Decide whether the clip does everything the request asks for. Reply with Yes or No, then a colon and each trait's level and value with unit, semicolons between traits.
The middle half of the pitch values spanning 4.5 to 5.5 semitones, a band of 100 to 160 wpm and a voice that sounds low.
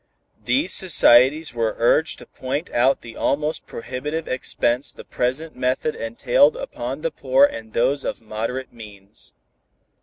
No: average, 4.0 semitones; average, 140 wpm; low, 130 Hz